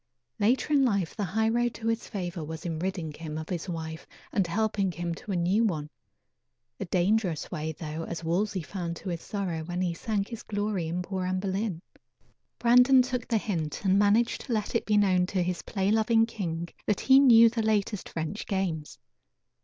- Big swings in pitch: No, average, 4.4 semitones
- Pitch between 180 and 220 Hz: Yes, high, 190 Hz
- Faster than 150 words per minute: Yes, average, 200 wpm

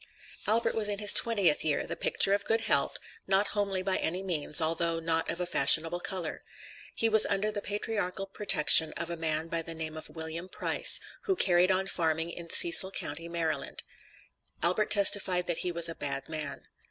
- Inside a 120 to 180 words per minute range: No, average, 190 wpm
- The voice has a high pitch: No, medium, 175 Hz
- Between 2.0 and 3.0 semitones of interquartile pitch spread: No, average, 3.5 semitones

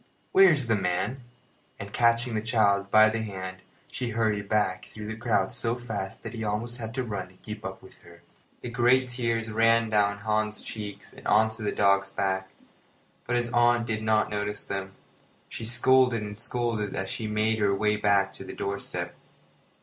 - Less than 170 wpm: No, average, 190 wpm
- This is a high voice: No, low, 110 Hz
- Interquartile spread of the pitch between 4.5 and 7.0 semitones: No, narrow, 2.5 semitones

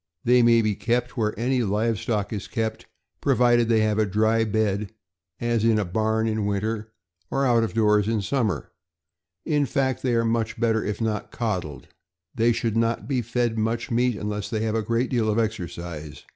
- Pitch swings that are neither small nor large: No, narrow, 1.8 semitones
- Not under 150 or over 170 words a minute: No, average, 185 wpm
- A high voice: No, low, 110 Hz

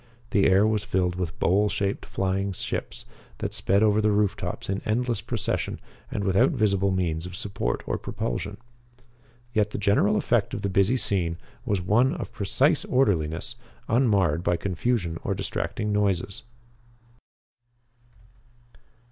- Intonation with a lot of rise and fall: No, narrow, 2.6 semitones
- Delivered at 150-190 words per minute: No, average, 140 wpm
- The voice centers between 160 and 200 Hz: No, low, 100 Hz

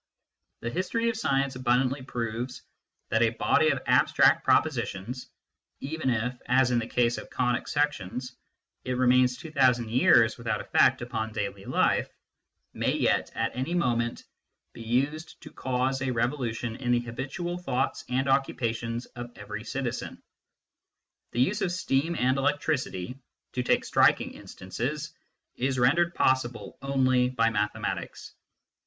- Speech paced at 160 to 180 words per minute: No, average, 145 wpm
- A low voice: Yes, low, 125 Hz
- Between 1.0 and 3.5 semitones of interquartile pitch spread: Yes, narrow, 2.5 semitones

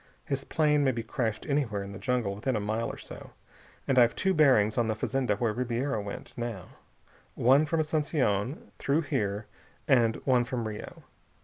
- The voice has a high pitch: No, low, 120 Hz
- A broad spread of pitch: No, average, 4.3 semitones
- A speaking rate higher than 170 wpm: Yes, average, 180 wpm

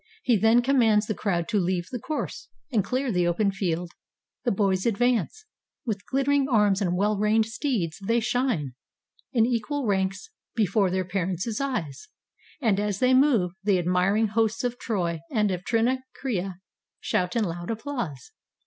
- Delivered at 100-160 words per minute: Yes, average, 155 wpm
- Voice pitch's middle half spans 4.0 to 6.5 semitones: Yes, average, 4.6 semitones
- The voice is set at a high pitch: Yes, high, 210 Hz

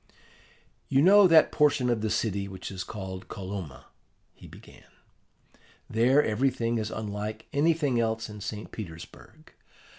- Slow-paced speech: Yes, slow, 130 wpm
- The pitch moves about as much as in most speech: Yes, average, 4.6 semitones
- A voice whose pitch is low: Yes, low, 110 Hz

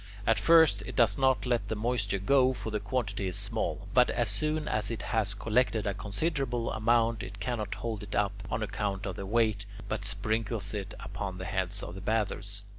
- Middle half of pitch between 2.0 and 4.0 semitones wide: Yes, average, 2.8 semitones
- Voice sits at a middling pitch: No, low, 105 Hz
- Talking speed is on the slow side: No, average, 200 wpm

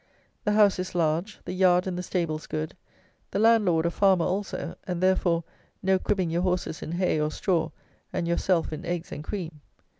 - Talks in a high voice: No, medium, 180 Hz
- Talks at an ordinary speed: Yes, average, 185 wpm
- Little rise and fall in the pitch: Yes, narrow, 2.3 semitones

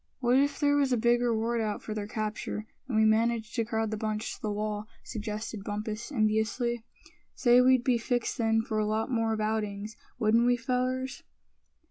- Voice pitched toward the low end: No, high, 225 Hz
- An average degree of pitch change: No, narrow, 2.1 semitones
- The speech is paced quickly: No, average, 190 wpm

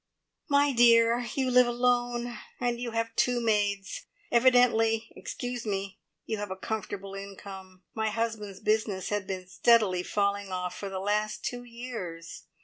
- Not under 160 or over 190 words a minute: No, average, 145 wpm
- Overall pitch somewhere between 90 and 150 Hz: No, high, 220 Hz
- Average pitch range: Yes, average, 3.4 semitones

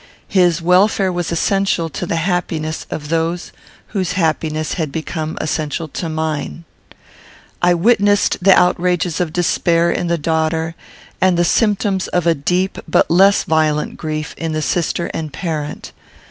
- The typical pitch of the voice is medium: Yes, medium, 170 Hz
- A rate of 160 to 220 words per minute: No, average, 145 wpm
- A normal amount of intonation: No, narrow, 2.3 semitones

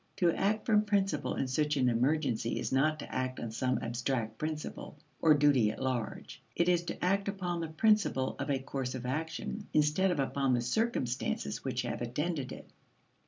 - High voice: No, medium, 145 Hz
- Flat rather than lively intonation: No, average, 5.2 semitones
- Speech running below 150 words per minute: No, average, 185 wpm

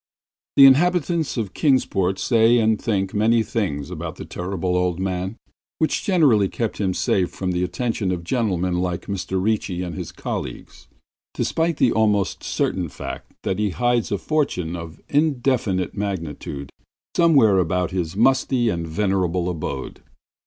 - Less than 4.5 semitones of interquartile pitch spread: No, average, 4.8 semitones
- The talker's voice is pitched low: Yes, low, 100 Hz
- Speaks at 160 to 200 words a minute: No, average, 145 wpm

